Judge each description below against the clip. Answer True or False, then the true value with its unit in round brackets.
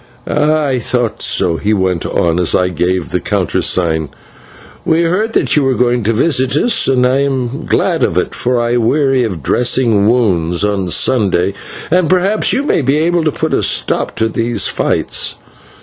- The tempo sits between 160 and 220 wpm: True (180 wpm)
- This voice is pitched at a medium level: False (120 Hz)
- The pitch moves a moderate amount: False (7.0 semitones)